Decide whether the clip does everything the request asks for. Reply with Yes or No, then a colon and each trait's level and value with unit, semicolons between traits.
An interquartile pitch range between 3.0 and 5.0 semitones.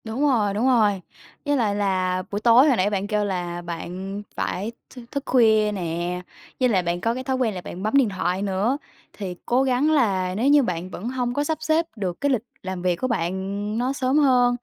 No: wide, 5.5 semitones